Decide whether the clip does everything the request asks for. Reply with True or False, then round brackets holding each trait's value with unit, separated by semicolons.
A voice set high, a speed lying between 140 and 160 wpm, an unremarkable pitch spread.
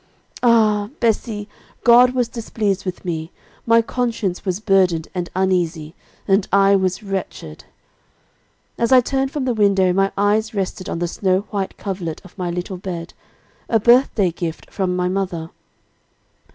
True (195 Hz; 150 wpm; 3.4 semitones)